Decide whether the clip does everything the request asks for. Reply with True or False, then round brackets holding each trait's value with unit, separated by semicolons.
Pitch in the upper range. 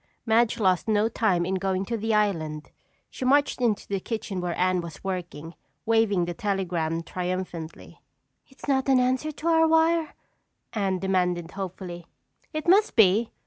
True (195 Hz)